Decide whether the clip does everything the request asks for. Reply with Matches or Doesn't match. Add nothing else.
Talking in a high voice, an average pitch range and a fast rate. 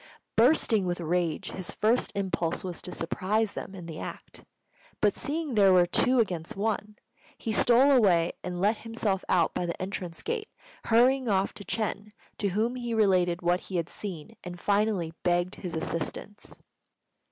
Doesn't match